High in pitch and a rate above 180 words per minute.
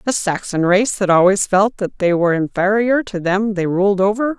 Yes: high, 195 Hz; fast, 205 wpm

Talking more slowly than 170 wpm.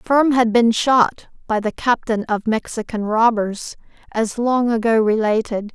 Yes: average, 145 wpm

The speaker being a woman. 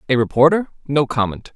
No: male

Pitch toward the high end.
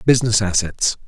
No: low, 105 Hz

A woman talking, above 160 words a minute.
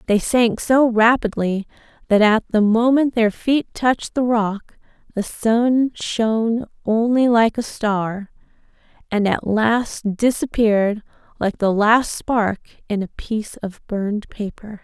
No: female; average, 140 wpm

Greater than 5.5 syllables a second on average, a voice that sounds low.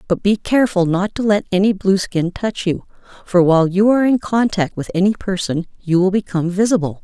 No: 5.7 syllables/s; high, 190 Hz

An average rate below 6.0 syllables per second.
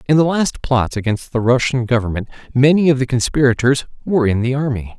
Yes: 5.8 syllables/s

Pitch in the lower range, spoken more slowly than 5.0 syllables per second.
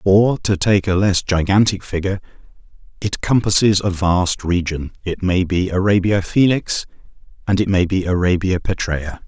Yes: very low, 95 Hz; 4.8 syllables/s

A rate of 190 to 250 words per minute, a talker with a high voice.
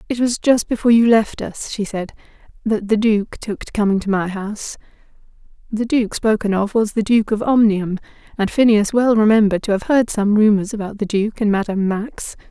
Yes: average, 200 wpm; high, 215 Hz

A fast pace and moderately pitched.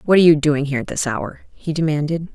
Yes: fast, 255 wpm; medium, 150 Hz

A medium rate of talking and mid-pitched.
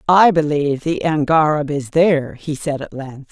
Yes: average, 180 wpm; medium, 150 Hz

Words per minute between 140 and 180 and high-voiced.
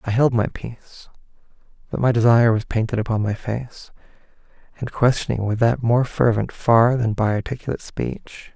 No: average, 160 wpm; low, 115 Hz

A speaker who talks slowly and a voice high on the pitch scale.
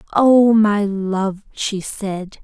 Yes: slow, 125 wpm; high, 205 Hz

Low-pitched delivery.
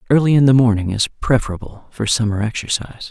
Yes: low, 115 Hz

